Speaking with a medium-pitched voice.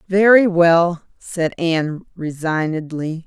Yes: medium, 170 Hz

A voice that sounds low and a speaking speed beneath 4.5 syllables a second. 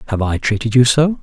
No: low, 125 Hz; 6.1 syllables/s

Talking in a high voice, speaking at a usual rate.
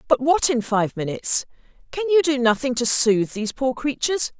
Yes: very high, 255 Hz; average, 190 wpm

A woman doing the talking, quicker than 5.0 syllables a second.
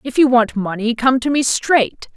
No: female; 4.5 syllables/s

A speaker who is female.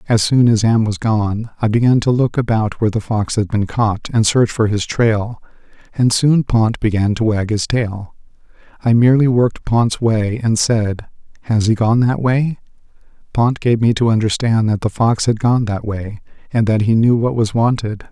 No: male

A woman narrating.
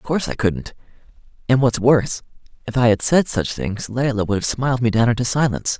No: male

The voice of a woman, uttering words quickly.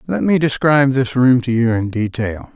No: male; fast, 210 wpm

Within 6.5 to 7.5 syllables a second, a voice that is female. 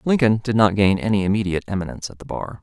No: 7.2 syllables/s; male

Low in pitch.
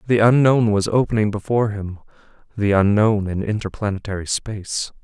Yes: low, 105 Hz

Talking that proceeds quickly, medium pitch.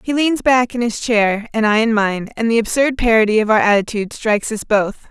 No: fast, 235 wpm; high, 225 Hz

